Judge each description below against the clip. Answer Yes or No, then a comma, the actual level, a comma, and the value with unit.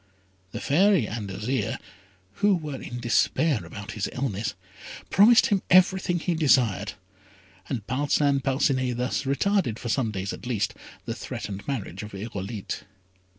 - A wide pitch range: Yes, wide, 6.2 semitones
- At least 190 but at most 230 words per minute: No, average, 140 wpm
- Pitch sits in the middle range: No, low, 125 Hz